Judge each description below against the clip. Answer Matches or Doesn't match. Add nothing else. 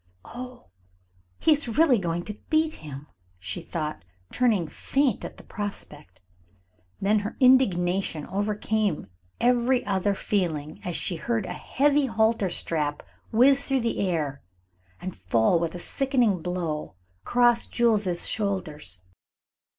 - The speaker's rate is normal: Doesn't match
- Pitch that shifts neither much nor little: Doesn't match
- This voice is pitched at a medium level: Doesn't match